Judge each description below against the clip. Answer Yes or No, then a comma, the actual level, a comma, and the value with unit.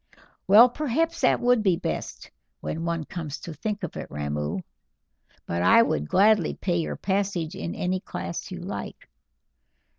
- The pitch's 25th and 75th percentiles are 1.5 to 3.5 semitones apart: No, average, 4.8 semitones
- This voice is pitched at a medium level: Yes, medium, 180 Hz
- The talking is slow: No, average, 155 wpm